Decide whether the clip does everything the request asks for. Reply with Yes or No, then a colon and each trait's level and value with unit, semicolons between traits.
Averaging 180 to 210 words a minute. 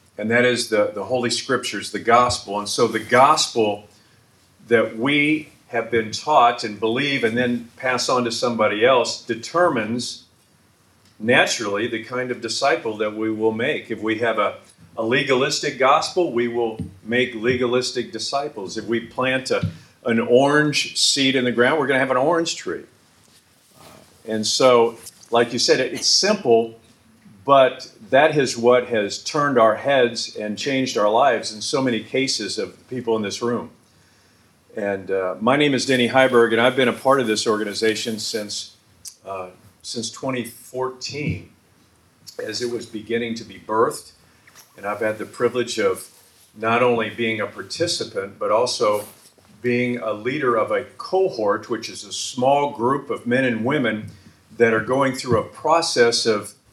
No: average, 165 wpm